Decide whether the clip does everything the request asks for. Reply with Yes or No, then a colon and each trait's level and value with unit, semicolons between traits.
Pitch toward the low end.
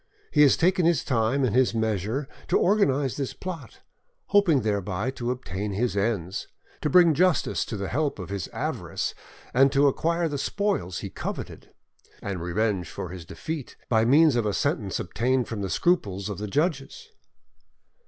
Yes: low, 125 Hz